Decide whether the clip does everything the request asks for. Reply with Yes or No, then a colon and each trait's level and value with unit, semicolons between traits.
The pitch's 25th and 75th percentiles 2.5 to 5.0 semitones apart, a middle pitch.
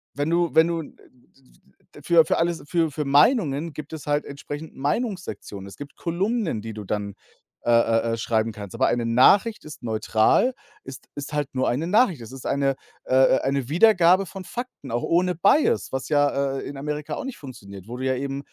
No: wide, 5.5 semitones; medium, 145 Hz